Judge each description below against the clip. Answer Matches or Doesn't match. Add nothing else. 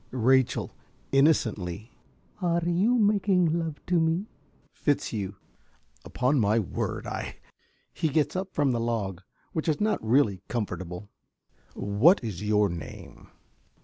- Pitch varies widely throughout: Matches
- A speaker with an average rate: Doesn't match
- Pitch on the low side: Matches